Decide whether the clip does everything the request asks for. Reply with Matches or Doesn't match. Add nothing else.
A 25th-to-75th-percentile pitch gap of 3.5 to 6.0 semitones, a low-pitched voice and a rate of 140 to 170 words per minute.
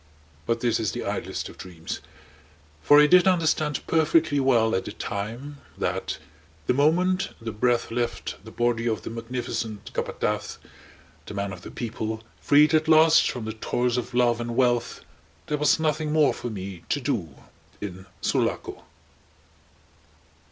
Matches